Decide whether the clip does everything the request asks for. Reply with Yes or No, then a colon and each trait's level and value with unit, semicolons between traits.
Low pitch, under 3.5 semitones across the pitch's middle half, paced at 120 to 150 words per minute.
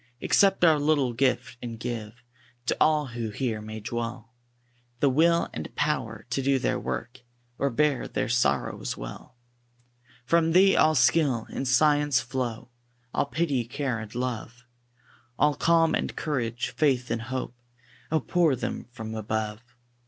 No: low, 125 Hz; average, 4.3 semitones; average, 145 wpm